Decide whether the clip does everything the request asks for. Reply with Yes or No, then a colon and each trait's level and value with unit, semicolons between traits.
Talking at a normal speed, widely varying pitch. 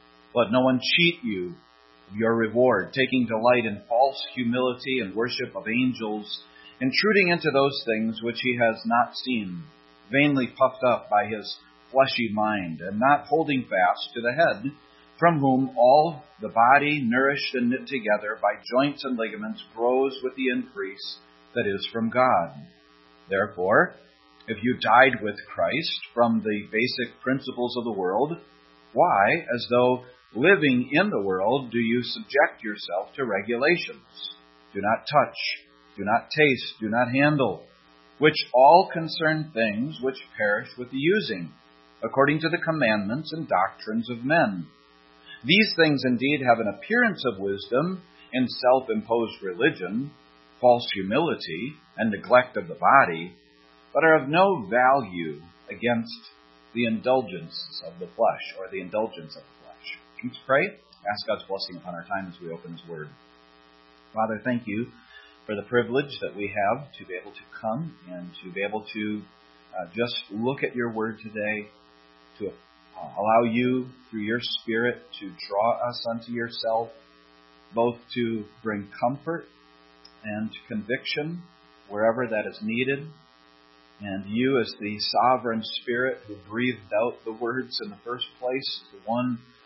Yes: average, 150 wpm; wide, 6.7 semitones